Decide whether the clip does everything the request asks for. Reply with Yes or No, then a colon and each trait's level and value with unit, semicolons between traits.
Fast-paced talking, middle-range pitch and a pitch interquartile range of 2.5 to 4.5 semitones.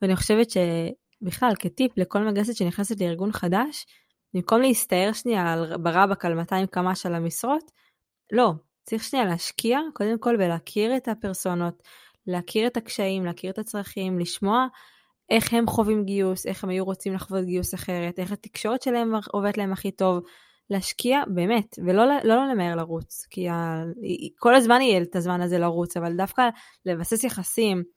No: fast, 160 wpm; high, 195 Hz; average, 4.2 semitones